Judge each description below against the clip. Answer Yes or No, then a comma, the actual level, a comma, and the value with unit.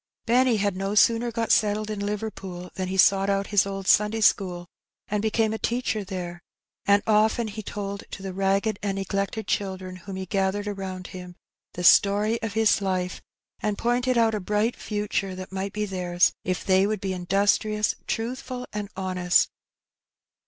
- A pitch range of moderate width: No, narrow, 2.2 semitones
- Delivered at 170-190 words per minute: Yes, average, 175 wpm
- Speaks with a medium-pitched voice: No, high, 200 Hz